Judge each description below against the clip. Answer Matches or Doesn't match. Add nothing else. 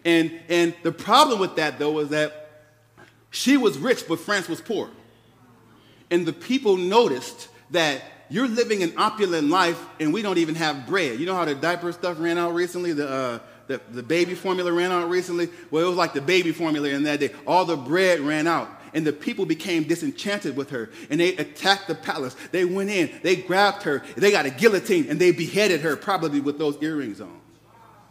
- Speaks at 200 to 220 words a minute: Matches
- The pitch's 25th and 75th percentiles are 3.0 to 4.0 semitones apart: Matches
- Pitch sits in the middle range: Matches